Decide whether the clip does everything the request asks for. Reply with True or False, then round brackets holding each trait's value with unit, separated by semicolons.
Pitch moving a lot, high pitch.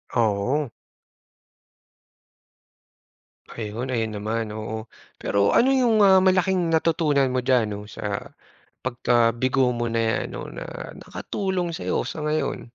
False (6.8 semitones; 130 Hz)